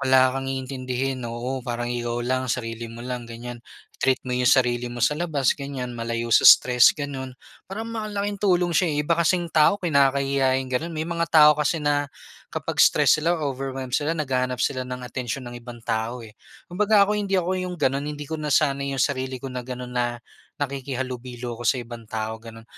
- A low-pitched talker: Yes, low, 130 Hz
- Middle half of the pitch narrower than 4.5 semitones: Yes, average, 3.6 semitones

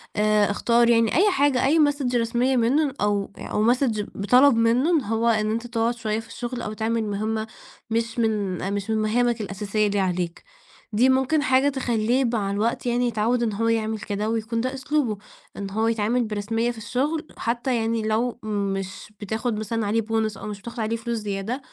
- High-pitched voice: Yes, high, 225 Hz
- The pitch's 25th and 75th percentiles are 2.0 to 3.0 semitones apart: Yes, narrow, 2.4 semitones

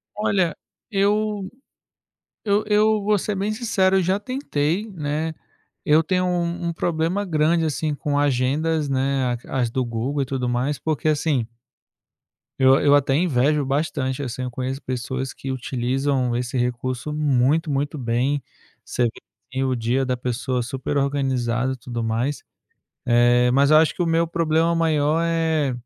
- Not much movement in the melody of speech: No, average, 4.4 semitones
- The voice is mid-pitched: Yes, medium, 145 Hz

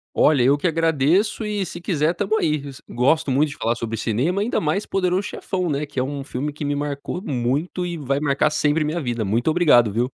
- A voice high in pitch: No, medium, 150 Hz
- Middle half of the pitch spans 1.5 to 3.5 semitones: No, average, 4.6 semitones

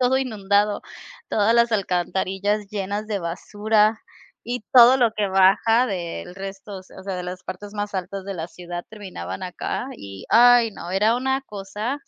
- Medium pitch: No, high, 205 Hz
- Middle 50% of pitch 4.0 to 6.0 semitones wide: No, average, 3.0 semitones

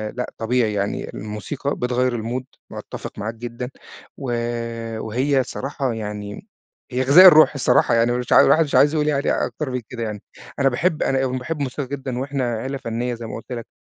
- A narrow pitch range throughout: No, average, 3.2 semitones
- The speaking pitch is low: Yes, low, 125 Hz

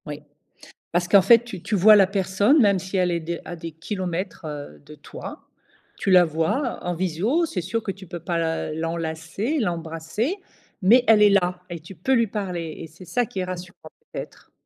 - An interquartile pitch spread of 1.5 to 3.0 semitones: No, average, 3.8 semitones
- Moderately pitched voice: Yes, medium, 180 Hz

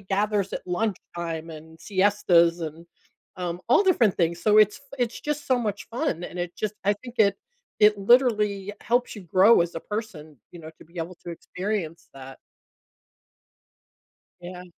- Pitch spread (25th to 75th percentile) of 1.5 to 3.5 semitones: No, average, 3.9 semitones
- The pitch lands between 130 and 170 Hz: No, high, 195 Hz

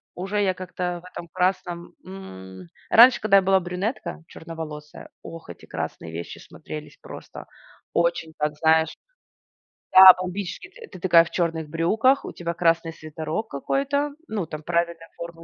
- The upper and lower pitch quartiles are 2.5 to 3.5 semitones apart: Yes, average, 2.9 semitones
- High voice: No, medium, 170 Hz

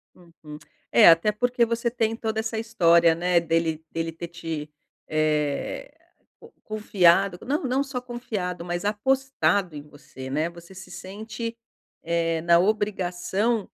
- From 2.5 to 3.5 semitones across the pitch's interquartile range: No, average, 5.1 semitones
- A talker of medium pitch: Yes, medium, 180 Hz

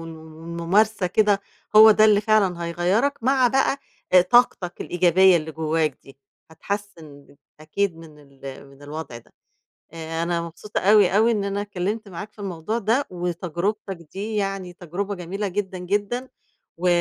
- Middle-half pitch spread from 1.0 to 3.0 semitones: No, average, 4.0 semitones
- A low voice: No, medium, 185 Hz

